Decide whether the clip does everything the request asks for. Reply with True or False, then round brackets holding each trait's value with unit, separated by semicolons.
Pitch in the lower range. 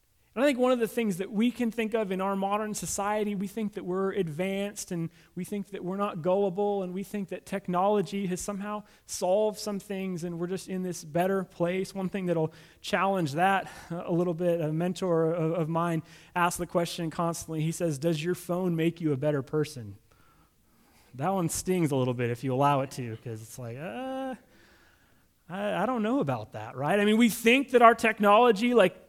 False (185 Hz)